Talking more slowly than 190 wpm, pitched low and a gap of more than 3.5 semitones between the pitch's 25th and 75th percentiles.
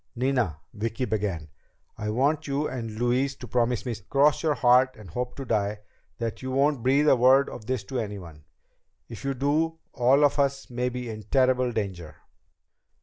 Yes: average, 180 wpm; low, 125 Hz; average, 4.0 semitones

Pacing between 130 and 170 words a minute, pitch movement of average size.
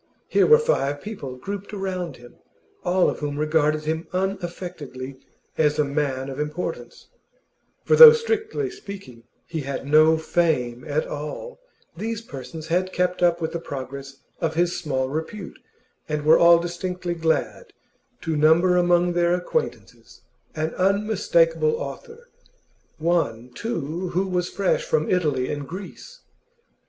Yes: average, 140 wpm; average, 3.8 semitones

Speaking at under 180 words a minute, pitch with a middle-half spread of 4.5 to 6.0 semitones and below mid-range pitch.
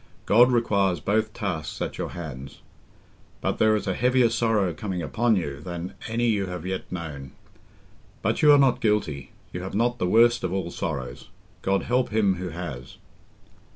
Yes: average, 170 wpm; average, 5.0 semitones; very low, 95 Hz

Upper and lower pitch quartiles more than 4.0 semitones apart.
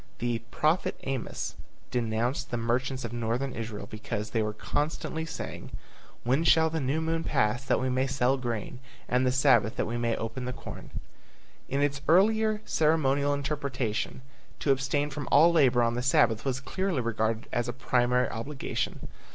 No: average, 3.4 semitones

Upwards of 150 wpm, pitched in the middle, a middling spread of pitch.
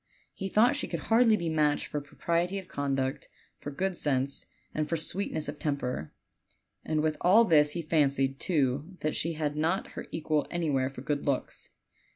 Yes: average, 180 wpm; medium, 155 Hz; average, 3.3 semitones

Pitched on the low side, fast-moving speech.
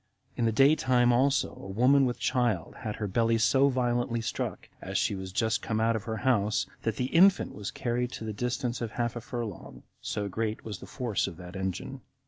Yes: low, 115 Hz; fast, 215 wpm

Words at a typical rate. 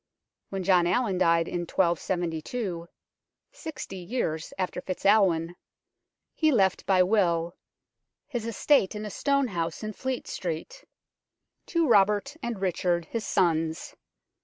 No: slow, 125 wpm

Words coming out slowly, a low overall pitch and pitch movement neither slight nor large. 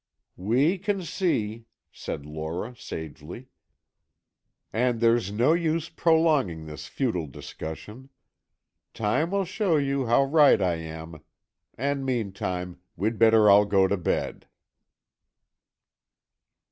No: slow, 110 wpm; low, 115 Hz; wide, 7.9 semitones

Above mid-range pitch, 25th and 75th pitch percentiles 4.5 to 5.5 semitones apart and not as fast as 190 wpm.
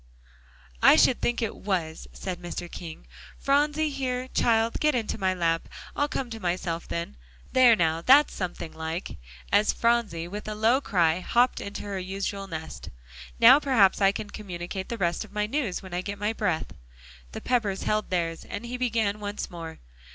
Yes: high, 205 Hz; average, 5.2 semitones; average, 180 wpm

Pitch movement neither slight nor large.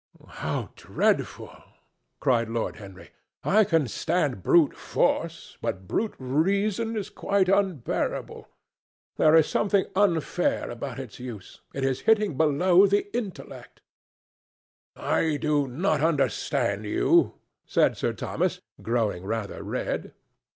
No: wide, 8.1 semitones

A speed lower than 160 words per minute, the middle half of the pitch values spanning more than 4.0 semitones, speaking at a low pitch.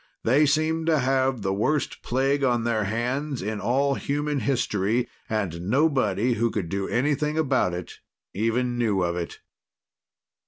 Yes: average, 150 wpm; average, 5.0 semitones; low, 125 Hz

